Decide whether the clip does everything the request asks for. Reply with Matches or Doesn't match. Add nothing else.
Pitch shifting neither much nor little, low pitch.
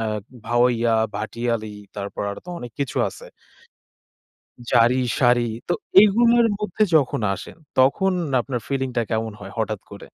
Matches